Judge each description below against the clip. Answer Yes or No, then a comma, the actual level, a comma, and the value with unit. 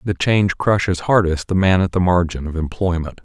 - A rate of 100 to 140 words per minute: No, fast, 205 wpm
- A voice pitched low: Yes, very low, 90 Hz